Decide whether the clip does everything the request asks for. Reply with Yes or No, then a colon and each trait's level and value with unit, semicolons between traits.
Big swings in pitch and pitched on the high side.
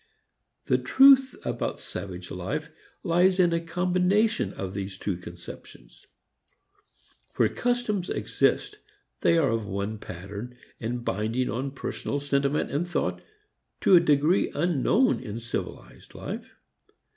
No: wide, 8.9 semitones; medium, 140 Hz